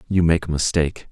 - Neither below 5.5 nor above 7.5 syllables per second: Yes, 6.5 syllables/s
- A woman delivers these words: No, male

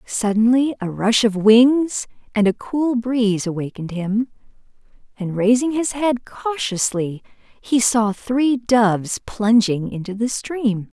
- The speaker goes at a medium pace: No, slow, 130 wpm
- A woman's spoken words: Yes, female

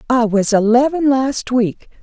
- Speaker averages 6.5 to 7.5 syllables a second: No, 4.1 syllables/s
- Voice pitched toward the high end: Yes, high, 245 Hz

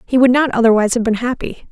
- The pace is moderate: No, fast, 245 wpm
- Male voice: No, female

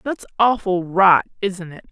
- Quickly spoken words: No, average, 155 wpm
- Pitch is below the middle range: No, high, 190 Hz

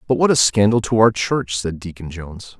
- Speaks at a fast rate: Yes, fast, 230 wpm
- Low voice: Yes, low, 100 Hz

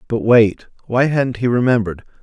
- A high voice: No, low, 120 Hz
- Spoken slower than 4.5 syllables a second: No, 5.2 syllables/s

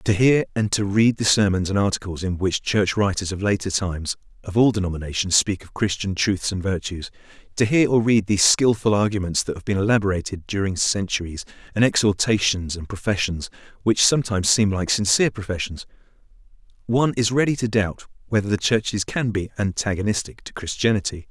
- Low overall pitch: Yes, low, 100 Hz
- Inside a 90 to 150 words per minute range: No, average, 170 wpm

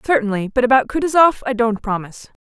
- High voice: Yes, high, 235 Hz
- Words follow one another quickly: No, average, 170 wpm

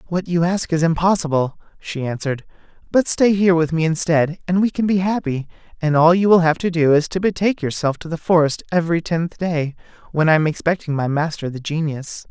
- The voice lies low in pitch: No, medium, 165 Hz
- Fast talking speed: Yes, fast, 210 wpm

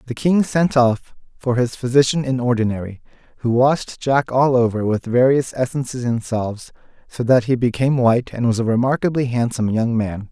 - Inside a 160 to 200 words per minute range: Yes, average, 180 wpm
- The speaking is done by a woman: No, male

